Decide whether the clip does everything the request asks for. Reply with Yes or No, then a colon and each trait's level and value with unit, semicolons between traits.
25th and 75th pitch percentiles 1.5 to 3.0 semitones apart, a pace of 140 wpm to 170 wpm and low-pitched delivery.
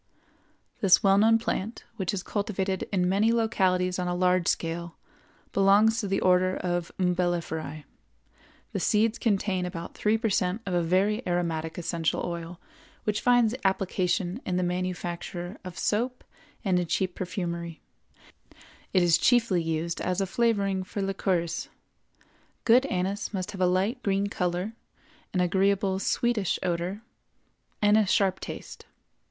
No: narrow, 2.5 semitones; average, 145 wpm; medium, 185 Hz